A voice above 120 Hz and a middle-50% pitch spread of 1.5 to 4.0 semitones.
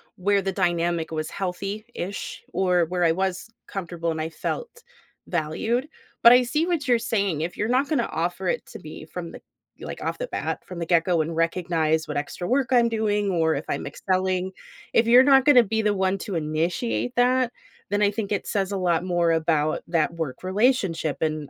No: medium, 185 Hz; wide, 5.5 semitones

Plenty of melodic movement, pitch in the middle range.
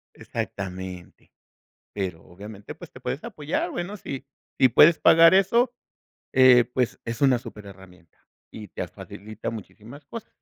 No: wide, 7.3 semitones; low, 115 Hz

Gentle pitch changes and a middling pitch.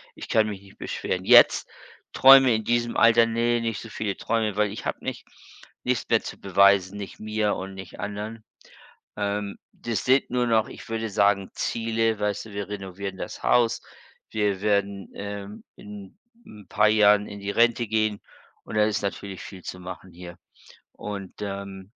No: narrow, 2.0 semitones; low, 105 Hz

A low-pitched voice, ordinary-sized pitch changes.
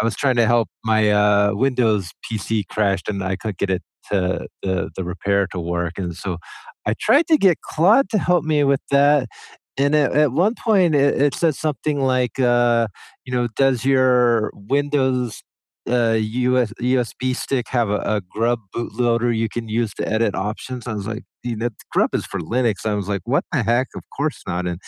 Yes: low, 120 Hz; average, 4.4 semitones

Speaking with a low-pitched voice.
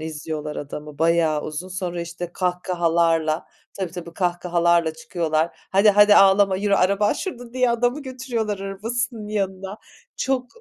No: medium, 185 Hz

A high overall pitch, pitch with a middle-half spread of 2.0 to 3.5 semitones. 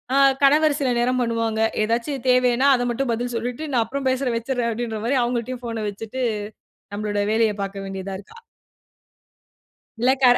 Yes: high, 240 Hz; narrow, 2.4 semitones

